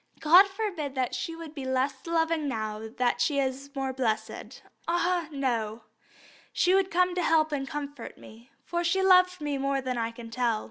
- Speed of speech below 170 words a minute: No, average, 185 wpm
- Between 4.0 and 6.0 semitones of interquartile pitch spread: Yes, average, 5.1 semitones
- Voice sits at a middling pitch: No, very high, 280 Hz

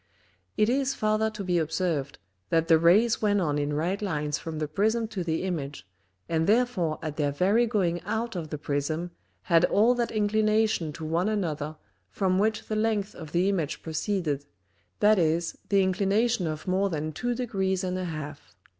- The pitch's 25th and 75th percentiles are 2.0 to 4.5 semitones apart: No, average, 5.2 semitones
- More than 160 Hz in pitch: Yes, medium, 185 Hz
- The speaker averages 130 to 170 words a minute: No, average, 180 wpm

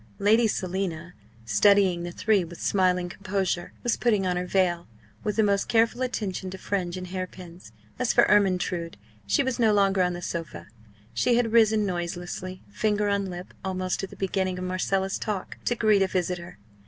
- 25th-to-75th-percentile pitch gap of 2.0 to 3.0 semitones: Yes, narrow, 2.5 semitones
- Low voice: No, high, 190 Hz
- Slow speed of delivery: No, average, 180 wpm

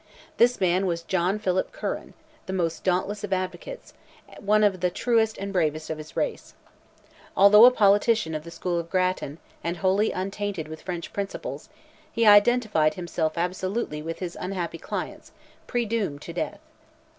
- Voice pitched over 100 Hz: Yes, medium, 185 Hz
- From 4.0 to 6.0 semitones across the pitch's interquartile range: No, average, 3.5 semitones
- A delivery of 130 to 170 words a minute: Yes, average, 155 wpm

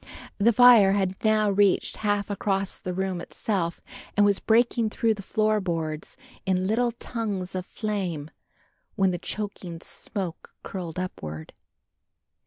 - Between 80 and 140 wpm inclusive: Yes, slow, 135 wpm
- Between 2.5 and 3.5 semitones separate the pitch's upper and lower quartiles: Yes, average, 2.8 semitones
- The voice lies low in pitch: No, high, 195 Hz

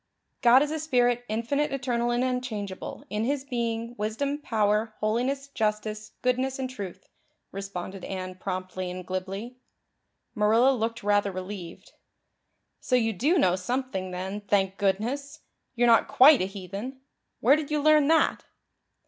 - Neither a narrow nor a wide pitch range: Yes, average, 4.8 semitones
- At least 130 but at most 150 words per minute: Yes, average, 140 wpm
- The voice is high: Yes, high, 225 Hz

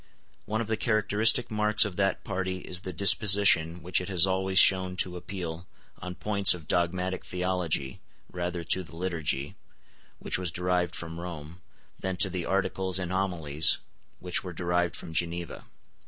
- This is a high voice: No, very low, 90 Hz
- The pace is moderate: Yes, average, 160 wpm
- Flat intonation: Yes, narrow, 1.8 semitones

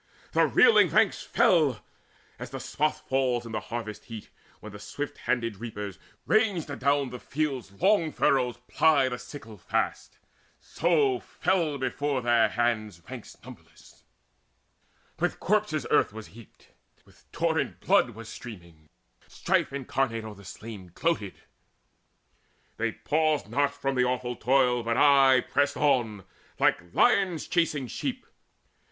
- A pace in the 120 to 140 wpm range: Yes, slow, 135 wpm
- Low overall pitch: Yes, low, 125 Hz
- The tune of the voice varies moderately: Yes, average, 4.5 semitones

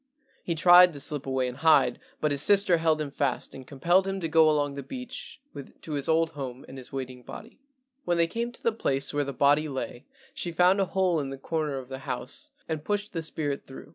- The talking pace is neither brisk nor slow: No, fast, 230 wpm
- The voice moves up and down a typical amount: Yes, average, 4.4 semitones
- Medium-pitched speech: Yes, medium, 155 Hz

